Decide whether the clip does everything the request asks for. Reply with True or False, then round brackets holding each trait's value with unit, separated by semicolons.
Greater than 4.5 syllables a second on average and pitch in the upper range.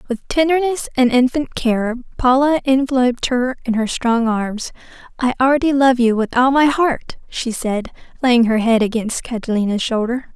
True (5.0 syllables/s; 250 Hz)